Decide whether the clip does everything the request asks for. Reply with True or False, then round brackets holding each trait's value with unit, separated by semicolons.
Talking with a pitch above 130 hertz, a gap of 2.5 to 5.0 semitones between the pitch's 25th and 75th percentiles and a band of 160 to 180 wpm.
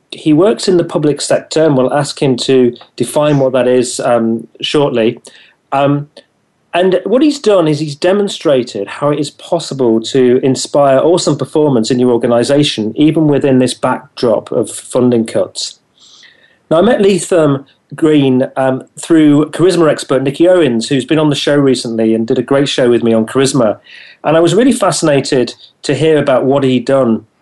True (140 Hz; 3.8 semitones; 175 wpm)